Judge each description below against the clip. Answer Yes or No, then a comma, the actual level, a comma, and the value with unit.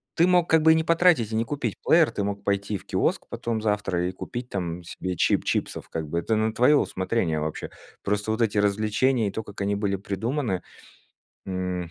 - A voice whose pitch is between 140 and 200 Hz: No, low, 105 Hz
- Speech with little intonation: No, average, 4.5 semitones